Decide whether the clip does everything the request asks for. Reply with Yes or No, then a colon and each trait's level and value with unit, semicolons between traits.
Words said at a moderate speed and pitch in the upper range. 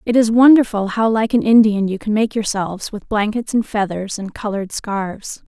Yes: average, 195 wpm; high, 215 Hz